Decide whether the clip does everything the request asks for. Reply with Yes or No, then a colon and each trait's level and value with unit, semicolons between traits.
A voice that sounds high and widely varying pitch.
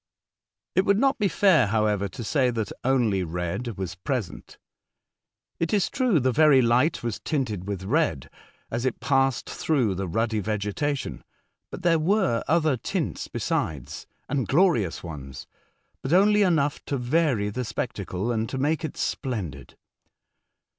No: low, 125 Hz; wide, 7.3 semitones